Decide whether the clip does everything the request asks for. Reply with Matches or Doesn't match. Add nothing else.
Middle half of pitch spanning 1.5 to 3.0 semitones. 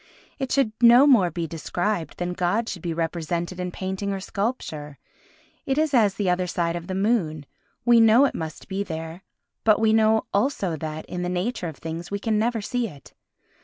Doesn't match